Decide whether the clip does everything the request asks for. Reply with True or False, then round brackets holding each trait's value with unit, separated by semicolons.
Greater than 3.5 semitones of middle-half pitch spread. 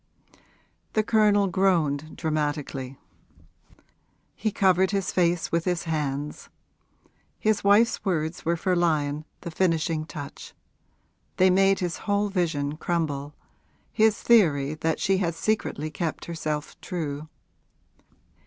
True (4.0 semitones)